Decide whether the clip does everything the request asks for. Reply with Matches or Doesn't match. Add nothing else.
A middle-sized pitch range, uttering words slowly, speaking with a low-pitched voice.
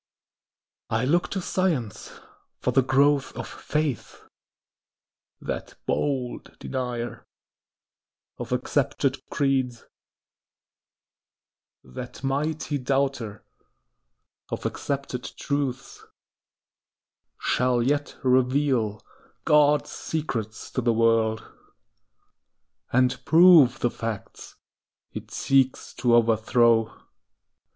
Matches